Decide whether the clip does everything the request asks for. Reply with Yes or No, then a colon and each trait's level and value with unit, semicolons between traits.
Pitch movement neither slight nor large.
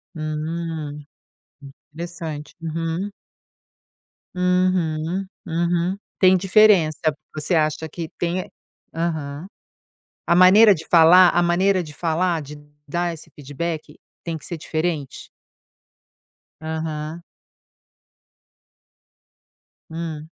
No: narrow, 2.2 semitones